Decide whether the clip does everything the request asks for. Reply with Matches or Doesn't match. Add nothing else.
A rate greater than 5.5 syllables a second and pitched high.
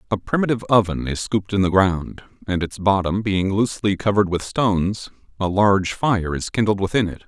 Doesn't match